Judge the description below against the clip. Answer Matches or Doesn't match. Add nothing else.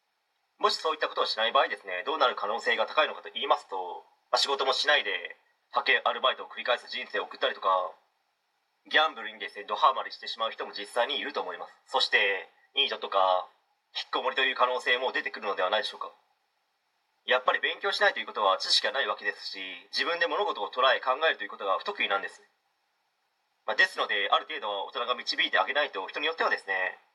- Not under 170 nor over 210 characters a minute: Doesn't match